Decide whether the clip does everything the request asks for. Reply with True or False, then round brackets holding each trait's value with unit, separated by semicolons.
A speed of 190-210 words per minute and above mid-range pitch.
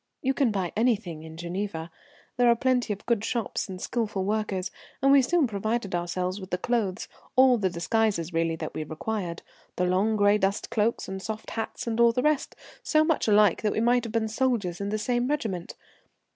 True (200 wpm; 210 Hz)